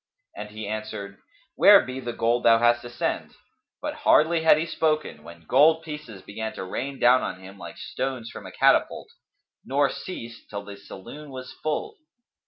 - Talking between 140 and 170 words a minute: No, average, 180 wpm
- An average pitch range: No, wide, 6.0 semitones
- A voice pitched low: Yes, low, 120 Hz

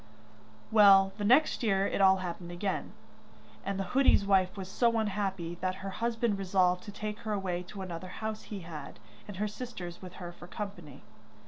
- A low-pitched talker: No, high, 195 Hz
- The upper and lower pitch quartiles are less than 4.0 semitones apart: Yes, narrow, 2.5 semitones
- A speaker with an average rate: Yes, average, 185 wpm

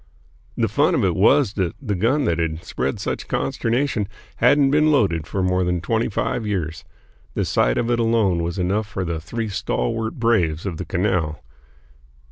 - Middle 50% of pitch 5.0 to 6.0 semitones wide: Yes, wide, 5.4 semitones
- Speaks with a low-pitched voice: Yes, very low, 95 Hz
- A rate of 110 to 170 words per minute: No, average, 180 wpm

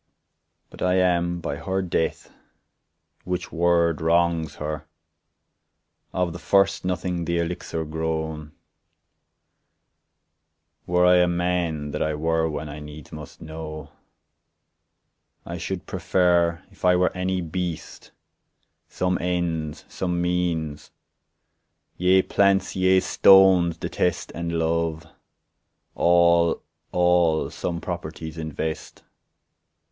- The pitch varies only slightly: Yes, narrow, 2.0 semitones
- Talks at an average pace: No, slow, 105 wpm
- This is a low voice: Yes, very low, 85 Hz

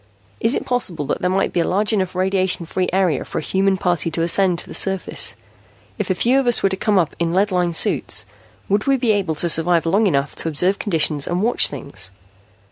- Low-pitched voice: No, medium, 185 Hz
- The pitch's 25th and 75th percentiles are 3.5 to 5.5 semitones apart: No, average, 3.1 semitones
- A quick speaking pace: Yes, fast, 230 wpm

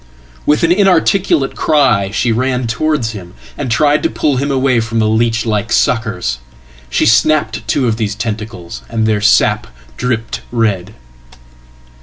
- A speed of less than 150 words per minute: Yes, average, 140 wpm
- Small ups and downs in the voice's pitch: No, average, 4.2 semitones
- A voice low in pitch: Yes, low, 115 Hz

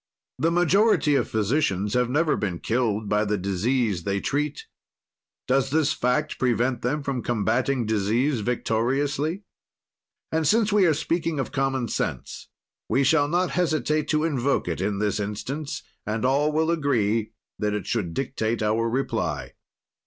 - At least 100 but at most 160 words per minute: Yes, average, 150 wpm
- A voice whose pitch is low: Yes, low, 130 Hz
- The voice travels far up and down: Yes, wide, 5.7 semitones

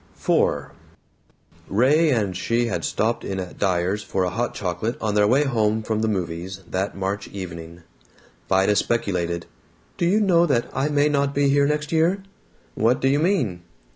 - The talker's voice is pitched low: Yes, low, 110 Hz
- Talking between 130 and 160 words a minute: No, average, 170 wpm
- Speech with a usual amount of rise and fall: No, wide, 6.9 semitones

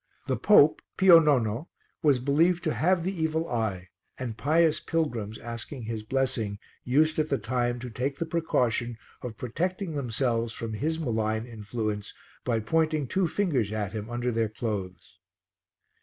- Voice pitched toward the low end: Yes, low, 125 Hz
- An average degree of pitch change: No, wide, 6.0 semitones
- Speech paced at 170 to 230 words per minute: No, average, 155 wpm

